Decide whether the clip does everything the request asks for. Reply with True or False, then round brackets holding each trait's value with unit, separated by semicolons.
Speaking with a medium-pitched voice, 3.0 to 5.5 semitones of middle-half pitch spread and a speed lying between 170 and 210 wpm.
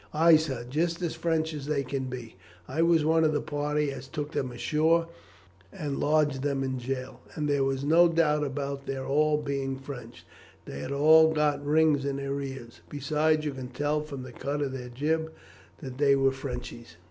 False (145 Hz; 2.5 semitones; 195 wpm)